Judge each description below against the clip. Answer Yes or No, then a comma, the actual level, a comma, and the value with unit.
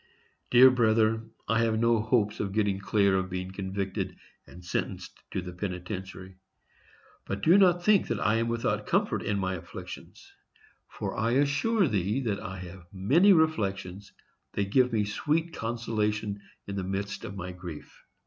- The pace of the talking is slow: No, average, 160 wpm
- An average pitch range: Yes, average, 3.6 semitones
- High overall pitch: No, low, 105 Hz